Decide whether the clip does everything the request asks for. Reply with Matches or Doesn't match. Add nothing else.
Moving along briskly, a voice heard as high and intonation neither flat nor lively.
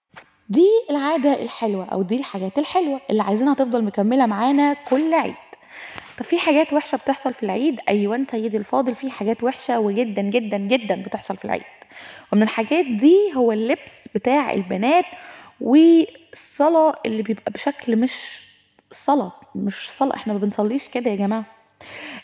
Matches